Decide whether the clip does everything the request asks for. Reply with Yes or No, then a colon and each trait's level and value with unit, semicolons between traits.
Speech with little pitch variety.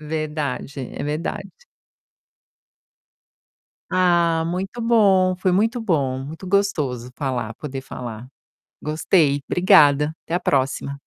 No: average, 5.0 semitones